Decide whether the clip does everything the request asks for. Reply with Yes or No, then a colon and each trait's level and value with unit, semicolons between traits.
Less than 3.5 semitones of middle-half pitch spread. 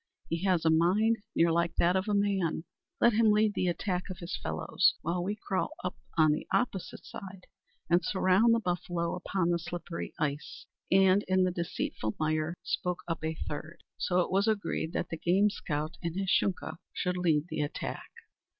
Yes: average, 2.7 semitones